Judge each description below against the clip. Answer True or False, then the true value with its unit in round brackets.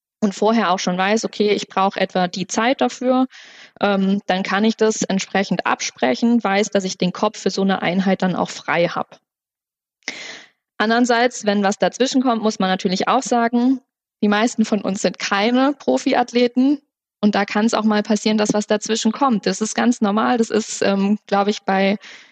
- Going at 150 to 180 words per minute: False (190 wpm)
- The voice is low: False (215 Hz)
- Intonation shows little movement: False (3.2 semitones)